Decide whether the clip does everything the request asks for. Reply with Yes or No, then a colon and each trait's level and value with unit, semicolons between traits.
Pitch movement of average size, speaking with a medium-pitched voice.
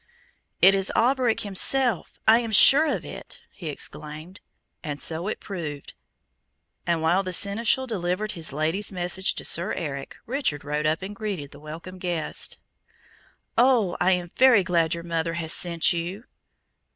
Yes: average, 4.5 semitones; medium, 180 Hz